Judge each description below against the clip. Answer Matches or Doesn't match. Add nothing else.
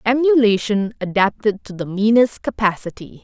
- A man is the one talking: Doesn't match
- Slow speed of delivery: Matches